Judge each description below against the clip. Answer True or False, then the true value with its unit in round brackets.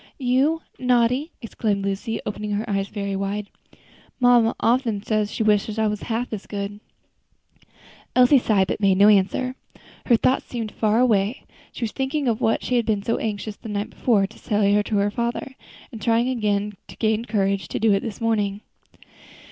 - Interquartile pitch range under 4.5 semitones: True (2.7 semitones)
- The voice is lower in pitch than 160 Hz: False (215 Hz)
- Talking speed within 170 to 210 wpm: True (180 wpm)